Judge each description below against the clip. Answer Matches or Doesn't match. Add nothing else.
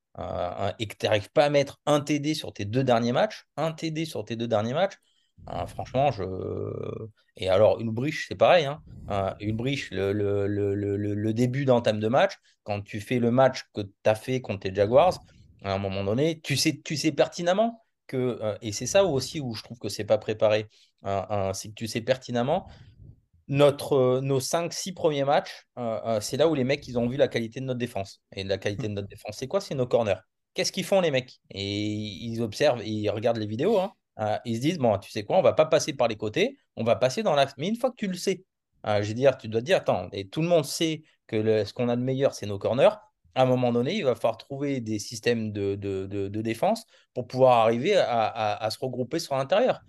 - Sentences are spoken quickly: Matches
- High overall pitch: Doesn't match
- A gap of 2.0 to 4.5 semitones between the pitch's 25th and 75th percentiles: Doesn't match